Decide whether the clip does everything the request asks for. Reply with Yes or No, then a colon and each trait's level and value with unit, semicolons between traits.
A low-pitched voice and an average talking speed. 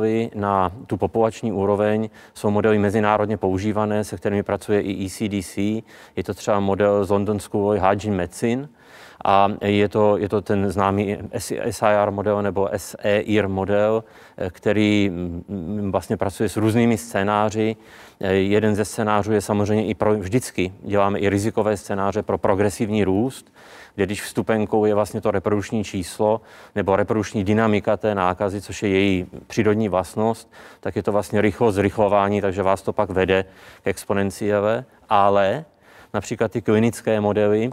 Yes: low, 105 Hz; average, 145 wpm